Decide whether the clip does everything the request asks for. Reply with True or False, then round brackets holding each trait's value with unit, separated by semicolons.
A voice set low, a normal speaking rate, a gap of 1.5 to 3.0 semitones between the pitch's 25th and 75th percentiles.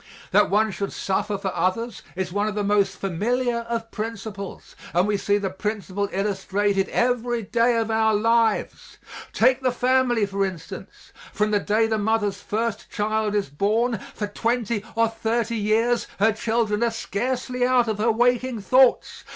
False (220 Hz; 165 wpm; 2.5 semitones)